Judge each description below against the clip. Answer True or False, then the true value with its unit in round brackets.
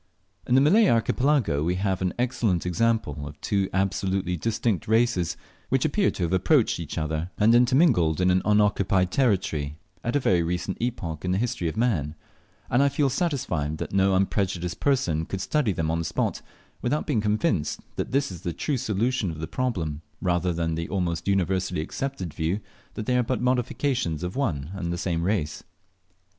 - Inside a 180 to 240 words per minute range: True (185 wpm)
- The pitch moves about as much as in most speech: False (6.3 semitones)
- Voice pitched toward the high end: False (95 Hz)